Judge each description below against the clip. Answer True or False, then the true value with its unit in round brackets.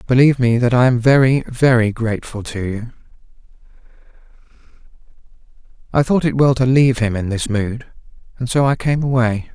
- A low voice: True (125 Hz)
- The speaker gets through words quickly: False (155 wpm)